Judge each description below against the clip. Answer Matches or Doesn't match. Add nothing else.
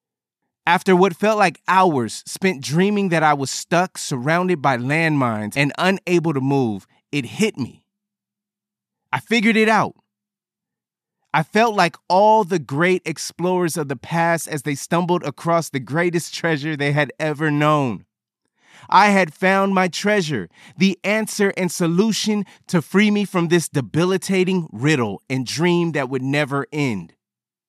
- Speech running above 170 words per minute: Doesn't match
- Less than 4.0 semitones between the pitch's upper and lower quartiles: Doesn't match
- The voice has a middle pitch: Matches